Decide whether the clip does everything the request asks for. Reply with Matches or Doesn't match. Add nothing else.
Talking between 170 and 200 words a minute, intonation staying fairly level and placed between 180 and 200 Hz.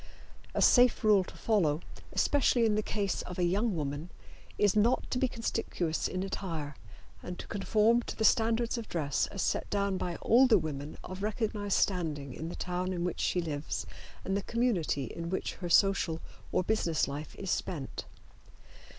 Doesn't match